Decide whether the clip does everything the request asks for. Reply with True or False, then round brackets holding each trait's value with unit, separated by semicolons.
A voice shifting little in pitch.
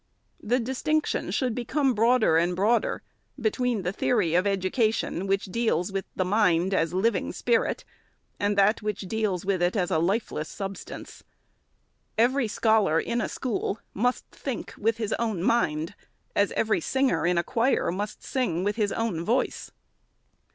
False (4.1 semitones)